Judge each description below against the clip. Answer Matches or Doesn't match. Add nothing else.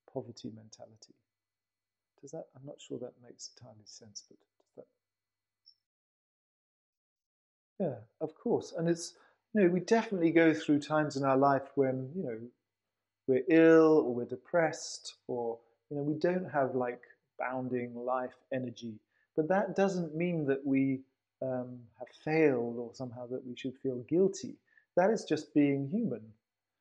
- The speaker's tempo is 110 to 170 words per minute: Matches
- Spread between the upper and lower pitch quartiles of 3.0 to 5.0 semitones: Doesn't match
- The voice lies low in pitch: Matches